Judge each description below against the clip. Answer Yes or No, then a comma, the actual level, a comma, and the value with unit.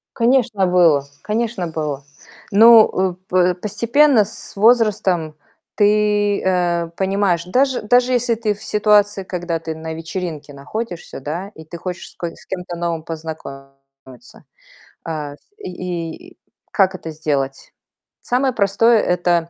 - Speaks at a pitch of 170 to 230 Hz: Yes, medium, 185 Hz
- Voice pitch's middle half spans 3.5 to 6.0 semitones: Yes, average, 4.6 semitones